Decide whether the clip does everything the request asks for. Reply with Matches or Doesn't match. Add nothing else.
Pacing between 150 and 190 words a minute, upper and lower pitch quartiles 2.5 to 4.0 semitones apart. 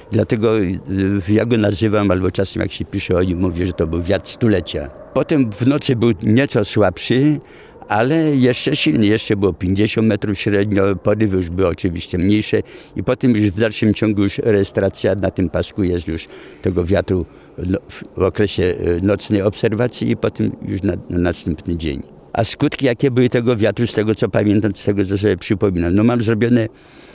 Matches